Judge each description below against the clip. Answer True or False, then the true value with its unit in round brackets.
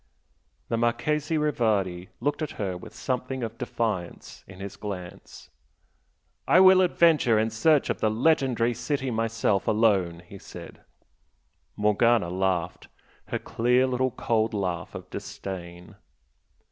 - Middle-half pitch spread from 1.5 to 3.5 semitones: False (5.0 semitones)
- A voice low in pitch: True (115 Hz)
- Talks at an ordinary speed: False (125 wpm)